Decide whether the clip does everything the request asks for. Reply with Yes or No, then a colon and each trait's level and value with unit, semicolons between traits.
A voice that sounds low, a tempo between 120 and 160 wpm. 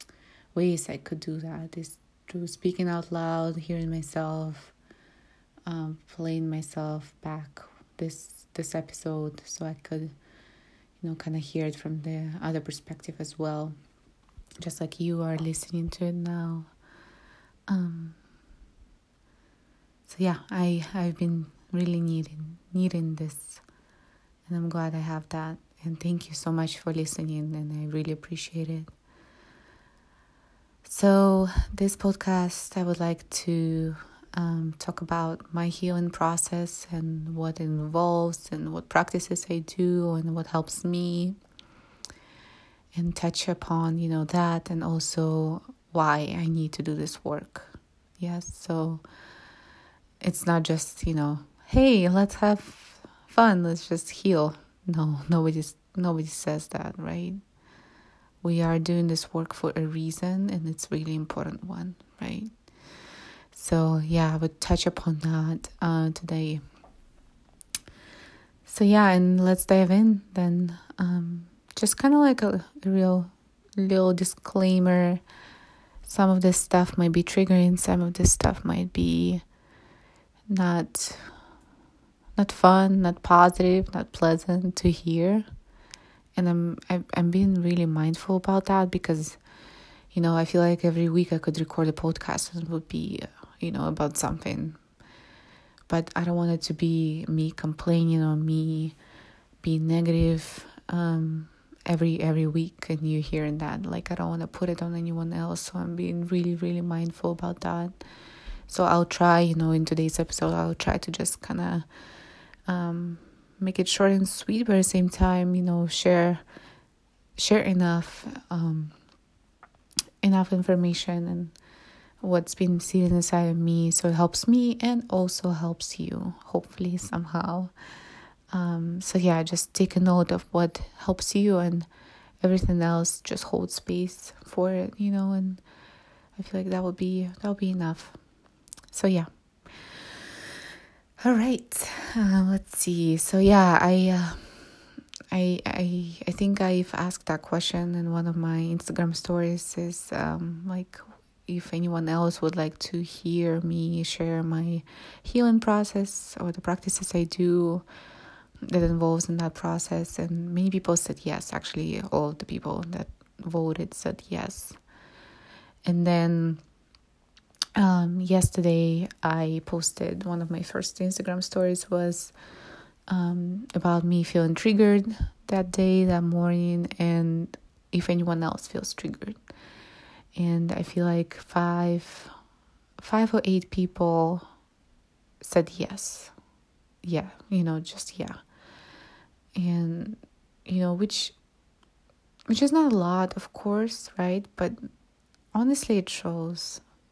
No: medium, 170 Hz; average, 140 wpm